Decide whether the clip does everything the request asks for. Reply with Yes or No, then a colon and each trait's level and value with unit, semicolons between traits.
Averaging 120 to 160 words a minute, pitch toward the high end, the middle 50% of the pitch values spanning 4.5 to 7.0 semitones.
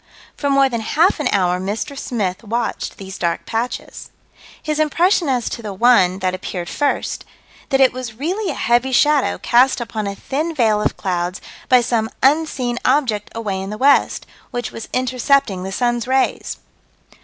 No: average, 170 wpm; high, 240 Hz; average, 5.0 semitones